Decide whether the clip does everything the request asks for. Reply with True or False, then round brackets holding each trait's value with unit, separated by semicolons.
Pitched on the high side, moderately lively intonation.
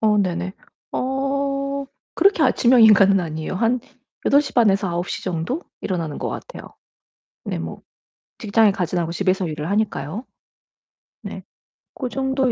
False (205 Hz; 7.0 semitones)